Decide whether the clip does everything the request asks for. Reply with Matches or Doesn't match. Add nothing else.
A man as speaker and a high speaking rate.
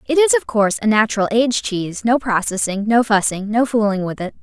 Doesn't match